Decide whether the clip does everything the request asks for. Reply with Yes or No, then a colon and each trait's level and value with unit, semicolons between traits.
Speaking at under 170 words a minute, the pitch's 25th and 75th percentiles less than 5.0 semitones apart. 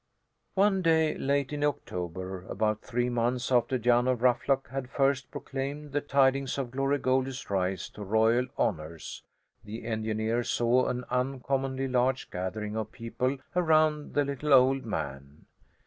Yes: average, 145 wpm; average, 3.7 semitones